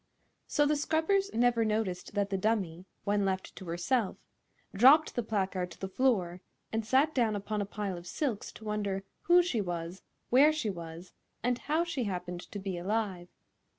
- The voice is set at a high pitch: Yes, high, 210 Hz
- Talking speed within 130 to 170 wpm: No, average, 180 wpm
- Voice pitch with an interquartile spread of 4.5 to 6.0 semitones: Yes, average, 5.0 semitones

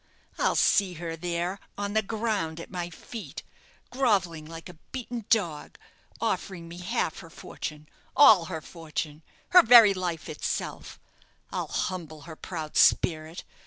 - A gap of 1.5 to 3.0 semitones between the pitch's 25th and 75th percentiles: No, average, 4.0 semitones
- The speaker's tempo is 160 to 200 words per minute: No, average, 140 wpm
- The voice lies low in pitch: No, medium, 175 Hz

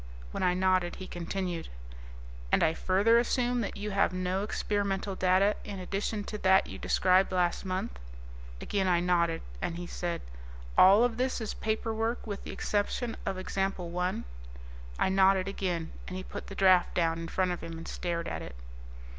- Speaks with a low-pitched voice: No, high, 190 Hz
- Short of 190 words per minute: Yes, average, 180 wpm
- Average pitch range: No, narrow, 2.3 semitones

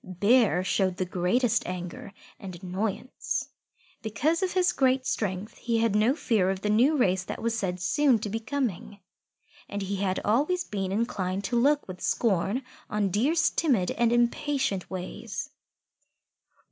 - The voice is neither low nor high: No, high, 215 Hz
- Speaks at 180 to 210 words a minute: No, average, 155 wpm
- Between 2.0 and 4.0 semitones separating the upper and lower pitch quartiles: No, average, 5.2 semitones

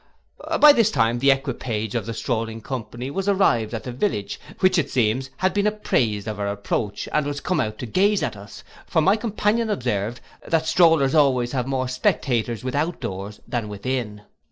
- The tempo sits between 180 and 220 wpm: Yes, average, 185 wpm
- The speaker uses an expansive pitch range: Yes, wide, 6.9 semitones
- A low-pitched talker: Yes, low, 130 Hz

